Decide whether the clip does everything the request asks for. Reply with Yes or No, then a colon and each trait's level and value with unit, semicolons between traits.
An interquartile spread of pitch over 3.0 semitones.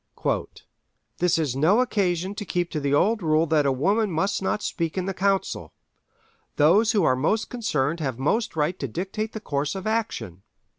Yes: wide, 5.5 semitones